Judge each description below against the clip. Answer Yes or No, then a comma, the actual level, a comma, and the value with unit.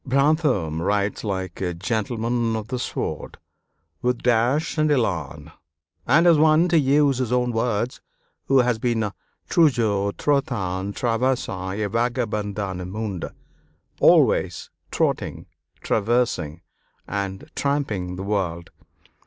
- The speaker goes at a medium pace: No, slow, 115 wpm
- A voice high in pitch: No, low, 115 Hz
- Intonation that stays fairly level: No, average, 4.6 semitones